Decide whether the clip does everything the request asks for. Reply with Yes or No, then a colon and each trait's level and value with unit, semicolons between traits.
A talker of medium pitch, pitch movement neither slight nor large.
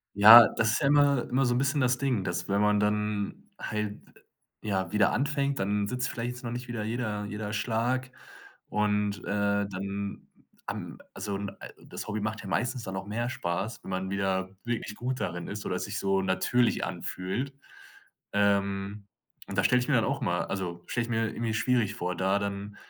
No: low, 105 Hz; average, 3.5 semitones